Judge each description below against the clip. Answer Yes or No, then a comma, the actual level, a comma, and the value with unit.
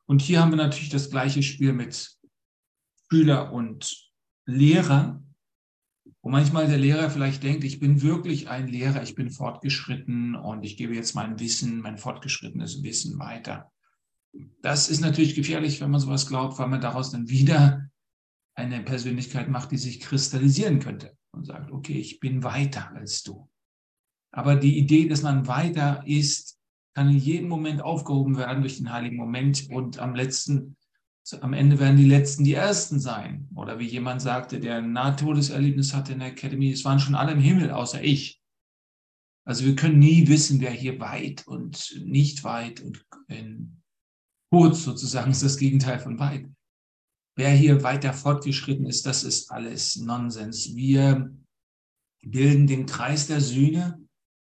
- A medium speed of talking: Yes, average, 160 wpm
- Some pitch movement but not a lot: No, narrow, 2.2 semitones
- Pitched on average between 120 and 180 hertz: Yes, medium, 140 Hz